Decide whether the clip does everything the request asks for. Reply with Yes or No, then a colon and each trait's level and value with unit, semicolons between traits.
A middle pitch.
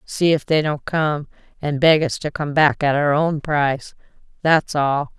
Yes: medium, 150 Hz